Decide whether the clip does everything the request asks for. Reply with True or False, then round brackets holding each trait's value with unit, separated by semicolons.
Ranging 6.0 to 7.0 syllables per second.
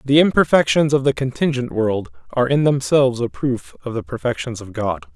False (5.5 syllables/s)